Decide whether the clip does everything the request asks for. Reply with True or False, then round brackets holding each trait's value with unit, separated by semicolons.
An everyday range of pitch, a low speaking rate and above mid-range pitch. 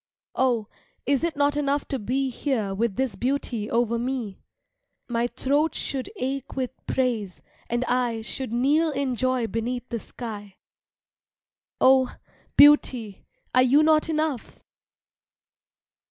True (3.0 semitones; 125 wpm; 255 Hz)